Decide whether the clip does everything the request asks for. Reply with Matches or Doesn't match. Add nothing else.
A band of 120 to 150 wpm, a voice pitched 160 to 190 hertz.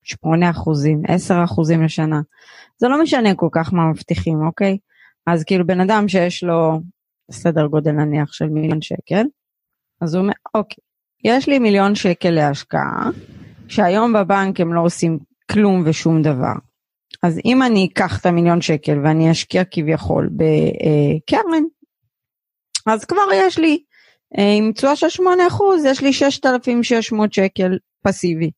Matches